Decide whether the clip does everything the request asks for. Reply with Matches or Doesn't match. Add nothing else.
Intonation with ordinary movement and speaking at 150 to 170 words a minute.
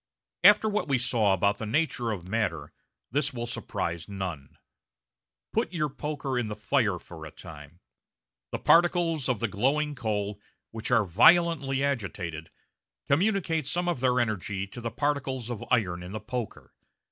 Doesn't match